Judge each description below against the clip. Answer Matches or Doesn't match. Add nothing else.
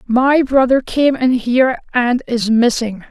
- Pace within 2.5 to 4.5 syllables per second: Matches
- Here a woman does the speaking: Matches